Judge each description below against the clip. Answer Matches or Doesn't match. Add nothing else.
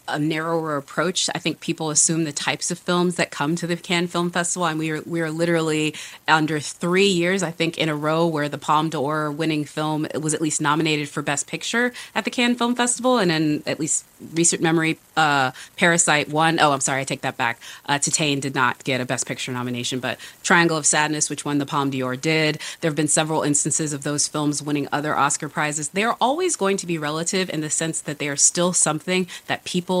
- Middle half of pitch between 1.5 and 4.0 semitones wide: Matches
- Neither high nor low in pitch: Matches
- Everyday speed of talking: Doesn't match